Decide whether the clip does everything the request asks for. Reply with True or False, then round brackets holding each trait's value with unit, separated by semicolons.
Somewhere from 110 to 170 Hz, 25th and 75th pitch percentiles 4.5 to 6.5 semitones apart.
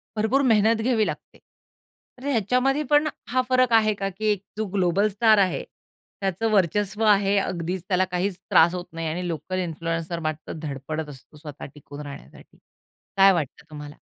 False (190 Hz; 4.8 semitones)